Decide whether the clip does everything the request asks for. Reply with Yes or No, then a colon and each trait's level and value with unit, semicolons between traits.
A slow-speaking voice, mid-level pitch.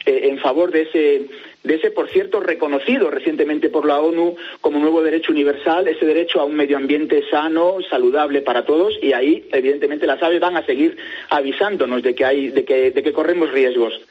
No: fast, 190 wpm; medium, 170 Hz